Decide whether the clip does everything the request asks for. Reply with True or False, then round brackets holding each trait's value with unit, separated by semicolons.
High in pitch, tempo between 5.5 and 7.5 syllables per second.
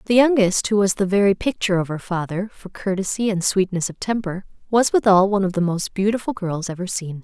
True (195 Hz; 5.9 syllables/s)